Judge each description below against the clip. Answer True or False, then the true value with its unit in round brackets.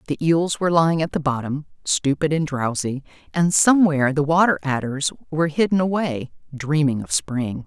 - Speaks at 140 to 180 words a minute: True (165 wpm)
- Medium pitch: True (150 Hz)